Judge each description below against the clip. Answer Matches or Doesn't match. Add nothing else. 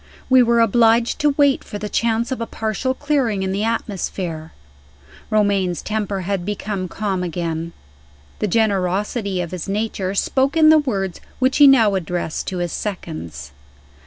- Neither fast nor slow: Matches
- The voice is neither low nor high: Doesn't match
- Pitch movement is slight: Doesn't match